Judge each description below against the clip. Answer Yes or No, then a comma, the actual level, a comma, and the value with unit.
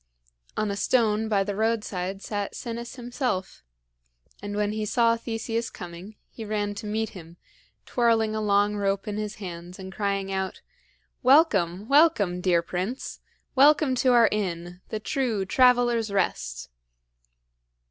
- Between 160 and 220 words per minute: No, average, 140 wpm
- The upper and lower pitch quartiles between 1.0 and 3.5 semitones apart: Yes, average, 3.2 semitones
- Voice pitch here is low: No, high, 210 Hz